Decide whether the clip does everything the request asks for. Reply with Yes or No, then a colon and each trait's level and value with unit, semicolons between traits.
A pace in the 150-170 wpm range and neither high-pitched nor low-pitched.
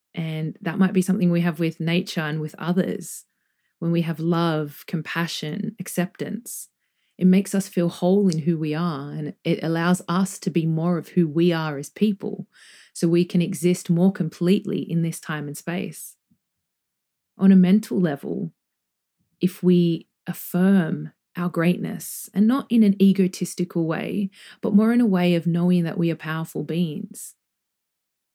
Yes: average, 165 wpm; medium, 175 Hz